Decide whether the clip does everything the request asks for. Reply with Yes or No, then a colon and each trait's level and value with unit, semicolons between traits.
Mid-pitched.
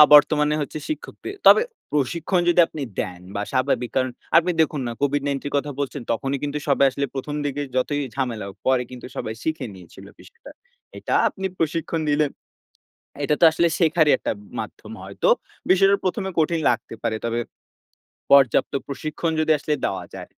Yes: medium, 145 Hz